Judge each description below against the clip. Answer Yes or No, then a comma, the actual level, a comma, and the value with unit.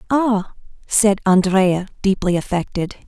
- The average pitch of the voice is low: No, high, 195 Hz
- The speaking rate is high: No, slow, 95 wpm